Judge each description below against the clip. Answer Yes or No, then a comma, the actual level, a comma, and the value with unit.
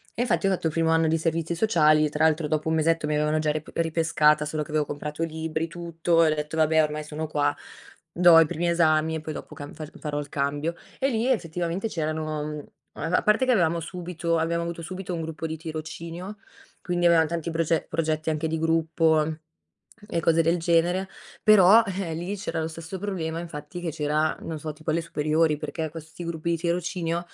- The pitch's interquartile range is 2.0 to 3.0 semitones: No, narrow, 1.6 semitones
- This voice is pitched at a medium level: Yes, medium, 160 Hz